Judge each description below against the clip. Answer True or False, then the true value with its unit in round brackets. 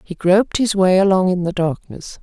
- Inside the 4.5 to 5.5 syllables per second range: True (5.2 syllables/s)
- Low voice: False (185 Hz)